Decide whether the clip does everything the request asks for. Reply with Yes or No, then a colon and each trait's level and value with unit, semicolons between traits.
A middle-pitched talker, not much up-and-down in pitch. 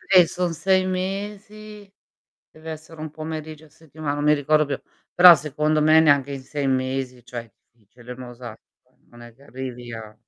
No: medium, 150 Hz; average, 4.0 semitones